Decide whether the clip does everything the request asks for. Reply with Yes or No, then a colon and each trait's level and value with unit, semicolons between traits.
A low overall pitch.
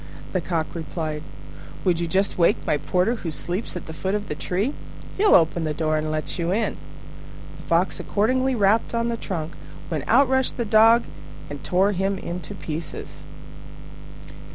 No: medium, 185 Hz